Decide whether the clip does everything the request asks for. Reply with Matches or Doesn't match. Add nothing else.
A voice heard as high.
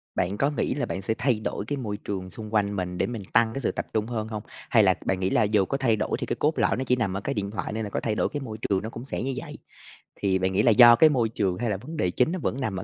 Doesn't match